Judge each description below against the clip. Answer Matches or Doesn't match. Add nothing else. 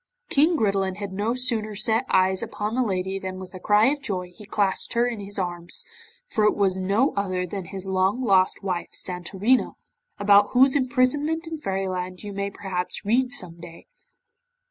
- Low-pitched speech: Doesn't match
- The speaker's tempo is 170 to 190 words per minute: Matches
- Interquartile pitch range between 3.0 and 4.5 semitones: Matches